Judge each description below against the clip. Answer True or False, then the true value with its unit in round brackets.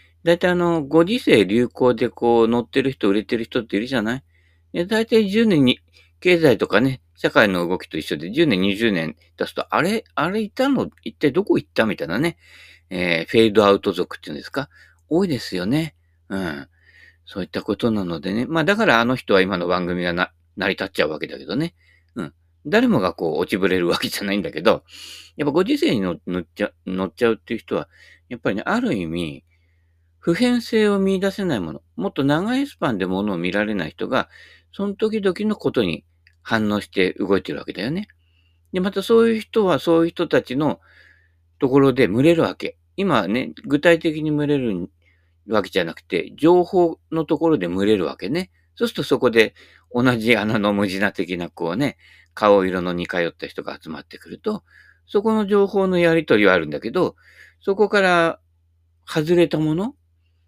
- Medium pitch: False (115 Hz)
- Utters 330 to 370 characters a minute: True (360 characters per minute)